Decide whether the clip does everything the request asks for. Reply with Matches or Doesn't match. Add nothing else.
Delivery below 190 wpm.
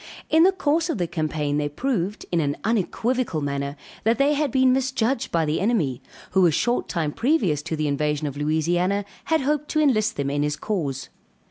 Doesn't match